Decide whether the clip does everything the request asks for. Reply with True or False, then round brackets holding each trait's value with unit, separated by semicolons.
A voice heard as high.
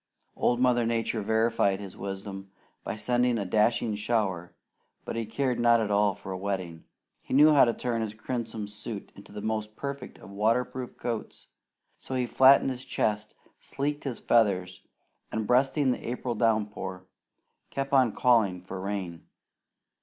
False (110 Hz)